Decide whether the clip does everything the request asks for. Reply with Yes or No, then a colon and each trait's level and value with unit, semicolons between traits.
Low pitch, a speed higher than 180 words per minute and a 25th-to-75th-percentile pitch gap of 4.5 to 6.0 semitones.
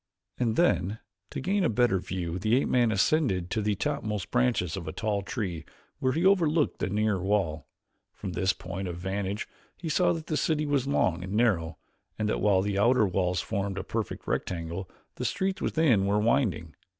Yes: low, 105 Hz; average, 190 wpm; wide, 5.6 semitones